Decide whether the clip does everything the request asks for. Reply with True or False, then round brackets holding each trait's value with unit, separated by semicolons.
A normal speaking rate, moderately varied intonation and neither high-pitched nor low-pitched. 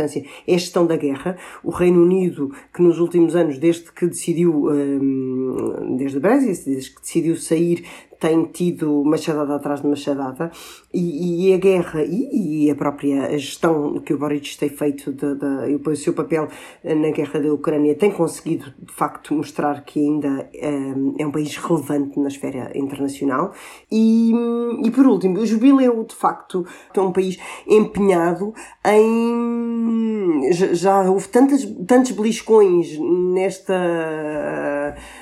True (145 wpm; 4.7 semitones; 165 Hz)